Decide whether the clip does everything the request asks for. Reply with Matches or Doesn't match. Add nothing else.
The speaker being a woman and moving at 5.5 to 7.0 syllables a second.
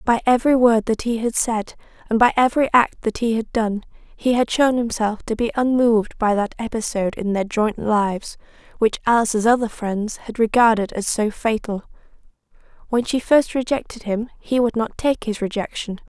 Doesn't match